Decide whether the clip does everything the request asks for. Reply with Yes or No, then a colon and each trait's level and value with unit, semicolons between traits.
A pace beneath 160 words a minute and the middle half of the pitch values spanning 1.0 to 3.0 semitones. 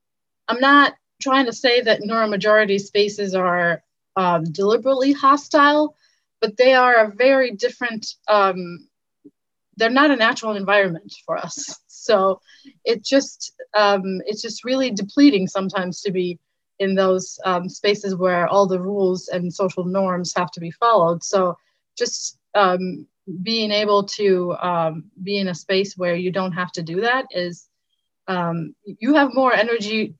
No: average, 150 wpm; average, 4.3 semitones